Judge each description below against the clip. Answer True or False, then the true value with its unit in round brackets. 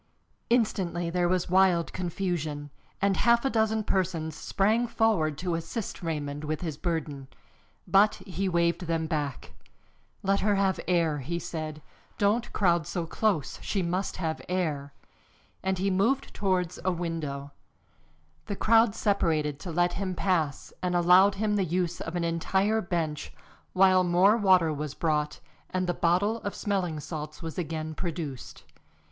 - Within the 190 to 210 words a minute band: False (150 wpm)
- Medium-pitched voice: True (175 Hz)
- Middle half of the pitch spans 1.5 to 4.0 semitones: True (3.5 semitones)